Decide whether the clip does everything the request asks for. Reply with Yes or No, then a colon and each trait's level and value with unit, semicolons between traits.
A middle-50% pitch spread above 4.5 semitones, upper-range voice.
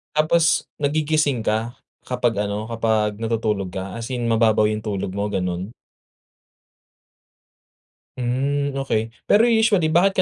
No: average, 5.1 semitones; low, 115 Hz